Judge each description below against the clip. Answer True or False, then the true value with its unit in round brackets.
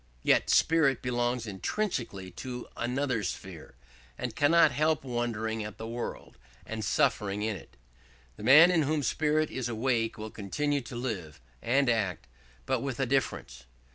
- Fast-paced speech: False (150 wpm)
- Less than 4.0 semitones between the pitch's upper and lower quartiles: False (4.3 semitones)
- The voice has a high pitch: False (120 Hz)